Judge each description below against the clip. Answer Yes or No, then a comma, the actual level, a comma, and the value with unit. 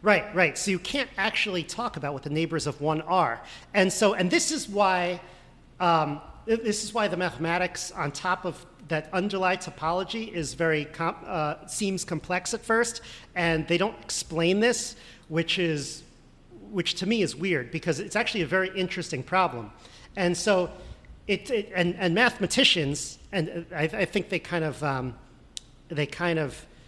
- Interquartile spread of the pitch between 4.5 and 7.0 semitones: No, average, 3.5 semitones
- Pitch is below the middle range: No, medium, 180 Hz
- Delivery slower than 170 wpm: No, average, 175 wpm